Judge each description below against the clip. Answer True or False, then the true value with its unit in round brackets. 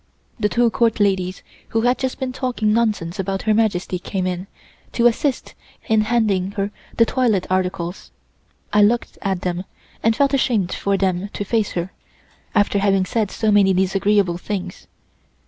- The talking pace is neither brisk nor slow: True (165 wpm)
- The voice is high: True (205 Hz)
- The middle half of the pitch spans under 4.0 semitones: True (3.3 semitones)